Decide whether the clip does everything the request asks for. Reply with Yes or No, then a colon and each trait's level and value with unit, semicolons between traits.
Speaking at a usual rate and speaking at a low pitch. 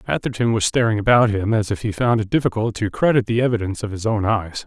No: fast, 245 wpm; low, 110 Hz